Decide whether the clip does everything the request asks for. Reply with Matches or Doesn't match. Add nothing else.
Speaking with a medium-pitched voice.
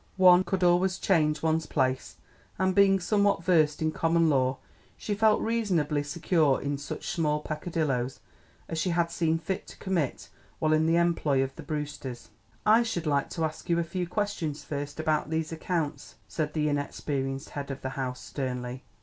Matches